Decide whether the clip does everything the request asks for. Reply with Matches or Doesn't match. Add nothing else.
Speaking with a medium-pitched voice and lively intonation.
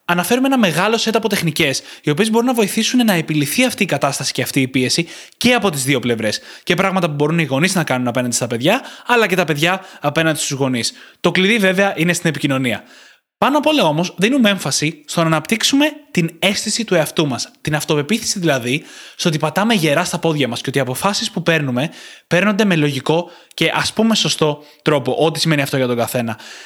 Matches